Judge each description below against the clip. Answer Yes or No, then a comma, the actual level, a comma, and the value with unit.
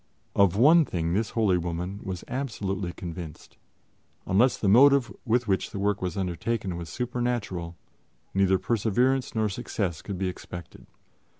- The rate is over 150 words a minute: No, average, 140 wpm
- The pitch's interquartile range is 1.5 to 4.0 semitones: No, average, 4.8 semitones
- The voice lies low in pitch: Yes, low, 100 Hz